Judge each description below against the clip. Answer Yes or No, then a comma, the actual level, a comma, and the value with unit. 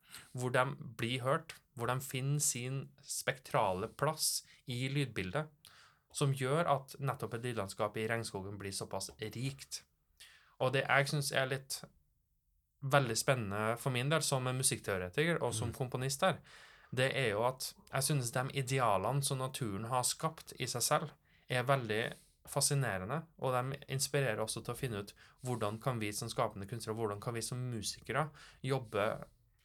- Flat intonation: No, average, 3.5 semitones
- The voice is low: Yes, low, 130 Hz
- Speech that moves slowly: No, average, 160 wpm